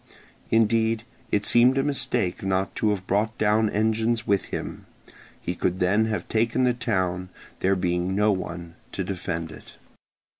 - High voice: No, low, 105 Hz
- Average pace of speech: Yes, average, 155 wpm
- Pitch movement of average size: Yes, average, 3.3 semitones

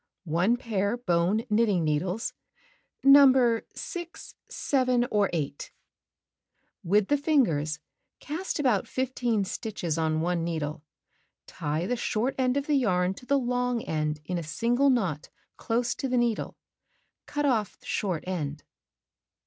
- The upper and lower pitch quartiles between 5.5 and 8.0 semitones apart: Yes, wide, 6.8 semitones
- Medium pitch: No, high, 215 Hz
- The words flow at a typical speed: No, slow, 130 wpm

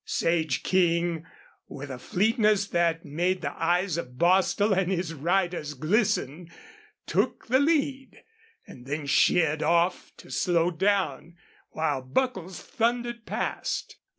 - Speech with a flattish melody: No, average, 4.1 semitones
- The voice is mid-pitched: Yes, medium, 175 Hz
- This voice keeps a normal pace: No, slow, 125 wpm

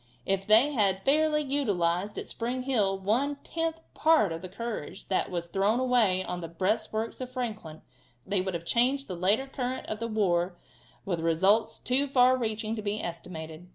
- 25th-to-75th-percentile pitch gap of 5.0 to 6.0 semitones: Yes, wide, 5.5 semitones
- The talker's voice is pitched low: No, high, 215 Hz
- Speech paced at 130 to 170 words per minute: No, average, 180 wpm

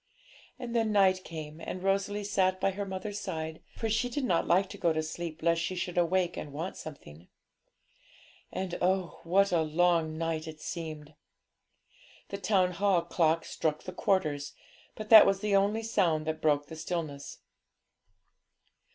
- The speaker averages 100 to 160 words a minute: No, average, 170 wpm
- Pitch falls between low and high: Yes, medium, 175 Hz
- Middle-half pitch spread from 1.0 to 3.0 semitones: No, average, 3.8 semitones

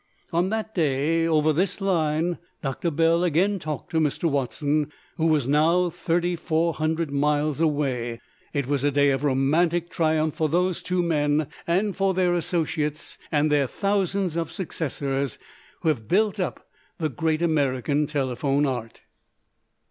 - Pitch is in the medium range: Yes, medium, 155 Hz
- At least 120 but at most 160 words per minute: Yes, average, 145 wpm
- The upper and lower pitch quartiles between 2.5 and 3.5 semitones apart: Yes, average, 3.2 semitones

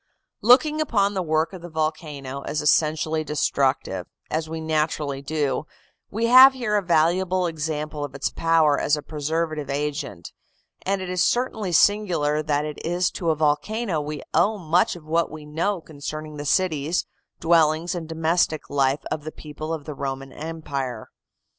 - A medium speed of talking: Yes, average, 165 wpm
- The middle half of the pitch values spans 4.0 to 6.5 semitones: No, average, 2.8 semitones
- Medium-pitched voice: Yes, medium, 155 Hz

